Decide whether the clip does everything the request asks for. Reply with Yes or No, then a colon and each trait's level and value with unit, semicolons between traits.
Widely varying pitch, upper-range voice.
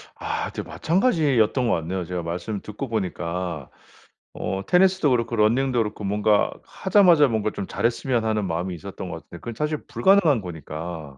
No: wide, 7.1 semitones; low, 110 Hz